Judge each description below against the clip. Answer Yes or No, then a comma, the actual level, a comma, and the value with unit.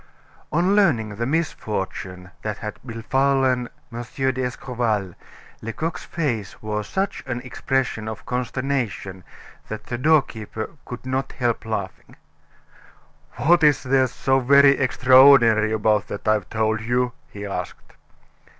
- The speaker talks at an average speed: No, slow, 120 wpm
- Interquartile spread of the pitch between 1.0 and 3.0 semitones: No, average, 3.6 semitones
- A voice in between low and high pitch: No, low, 120 Hz